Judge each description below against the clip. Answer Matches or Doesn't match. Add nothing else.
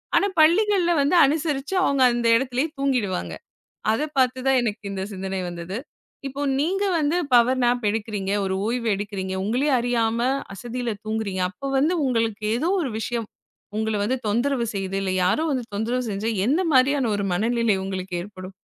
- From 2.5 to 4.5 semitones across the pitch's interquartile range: Doesn't match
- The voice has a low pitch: Doesn't match